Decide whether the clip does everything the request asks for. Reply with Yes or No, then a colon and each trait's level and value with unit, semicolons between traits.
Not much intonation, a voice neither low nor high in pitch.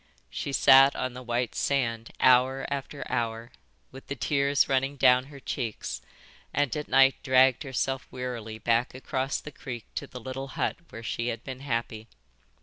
No: narrow, 2.3 semitones; low, 130 Hz